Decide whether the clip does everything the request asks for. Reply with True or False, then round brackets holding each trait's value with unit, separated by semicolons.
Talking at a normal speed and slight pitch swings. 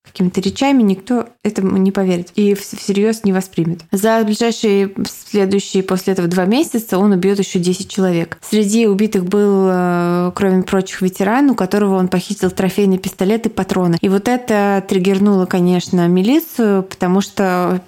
True (150 wpm; 2.0 semitones)